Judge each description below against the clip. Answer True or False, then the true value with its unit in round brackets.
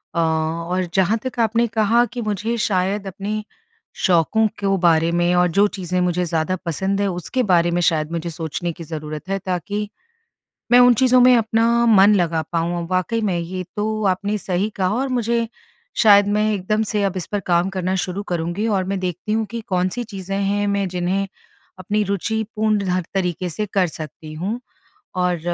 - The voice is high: True (195 Hz)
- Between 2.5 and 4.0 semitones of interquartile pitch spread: True (3.4 semitones)